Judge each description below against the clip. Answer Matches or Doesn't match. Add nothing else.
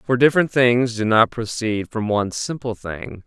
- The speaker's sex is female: Doesn't match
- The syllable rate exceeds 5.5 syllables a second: Doesn't match